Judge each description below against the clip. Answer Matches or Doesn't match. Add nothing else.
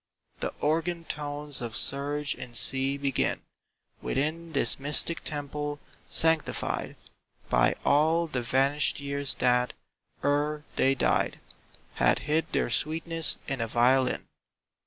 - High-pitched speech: Doesn't match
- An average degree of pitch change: Doesn't match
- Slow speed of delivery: Matches